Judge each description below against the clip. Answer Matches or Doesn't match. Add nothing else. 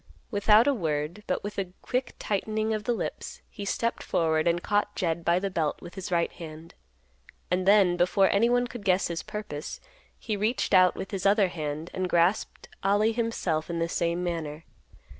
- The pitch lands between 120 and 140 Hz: Doesn't match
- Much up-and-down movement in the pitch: Doesn't match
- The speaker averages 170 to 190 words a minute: Matches